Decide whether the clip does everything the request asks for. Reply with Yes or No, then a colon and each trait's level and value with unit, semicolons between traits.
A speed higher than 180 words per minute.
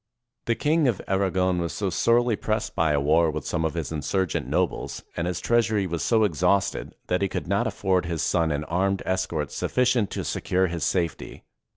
Yes: average, 200 wpm